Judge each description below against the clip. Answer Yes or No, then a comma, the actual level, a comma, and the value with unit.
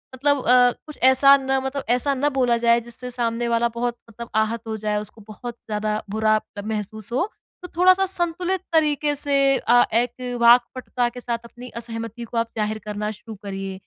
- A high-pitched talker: Yes, high, 240 Hz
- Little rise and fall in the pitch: No, average, 3.3 semitones